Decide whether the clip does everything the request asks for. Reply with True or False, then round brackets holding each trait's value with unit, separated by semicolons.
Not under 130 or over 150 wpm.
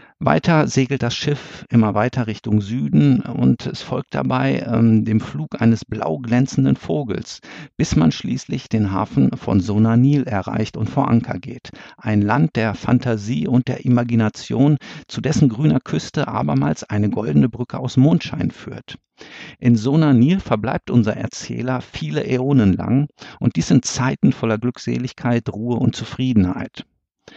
True (145 wpm)